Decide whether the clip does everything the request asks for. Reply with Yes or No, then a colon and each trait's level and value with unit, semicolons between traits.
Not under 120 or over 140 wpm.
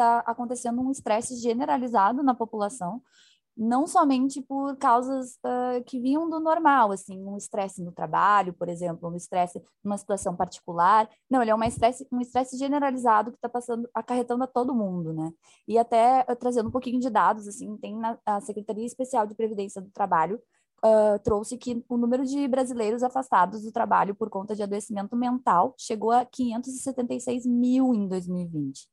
No: average, 170 wpm